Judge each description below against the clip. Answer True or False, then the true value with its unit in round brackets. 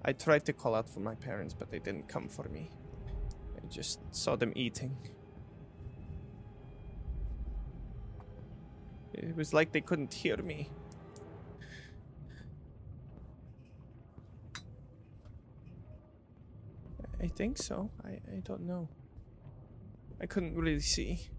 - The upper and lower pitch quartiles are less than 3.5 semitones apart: False (4.5 semitones)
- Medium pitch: False (115 Hz)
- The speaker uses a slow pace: True (105 wpm)